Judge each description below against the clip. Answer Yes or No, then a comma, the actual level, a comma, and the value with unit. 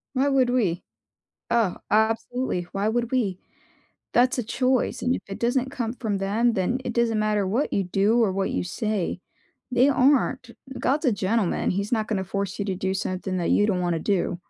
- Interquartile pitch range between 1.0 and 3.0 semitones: No, average, 4.2 semitones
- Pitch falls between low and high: No, high, 220 Hz